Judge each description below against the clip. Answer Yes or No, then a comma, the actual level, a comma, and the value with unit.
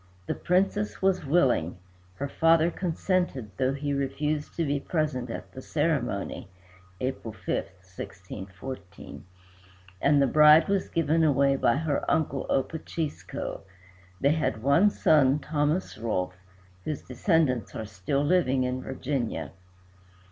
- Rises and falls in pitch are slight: No, average, 4.1 semitones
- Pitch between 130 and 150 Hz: Yes, medium, 140 Hz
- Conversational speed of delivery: No, slow, 125 wpm